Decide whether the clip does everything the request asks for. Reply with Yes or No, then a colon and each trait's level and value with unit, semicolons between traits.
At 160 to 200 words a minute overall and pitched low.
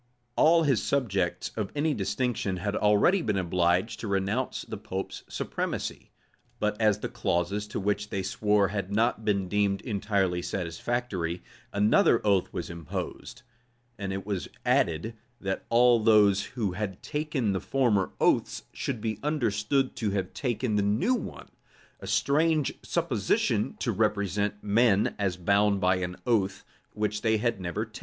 No: average, 150 wpm; low, 105 Hz